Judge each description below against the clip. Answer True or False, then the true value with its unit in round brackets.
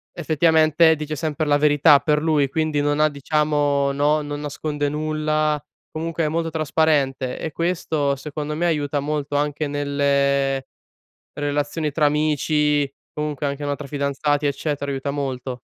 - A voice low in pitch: False (145 Hz)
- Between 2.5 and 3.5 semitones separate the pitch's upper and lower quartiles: False (1.4 semitones)